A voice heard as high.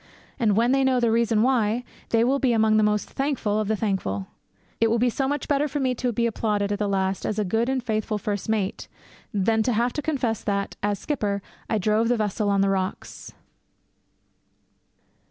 Yes: high, 220 Hz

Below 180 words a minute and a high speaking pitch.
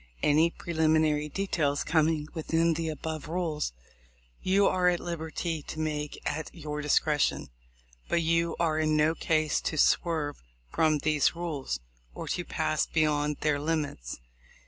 No: average, 140 wpm; medium, 155 Hz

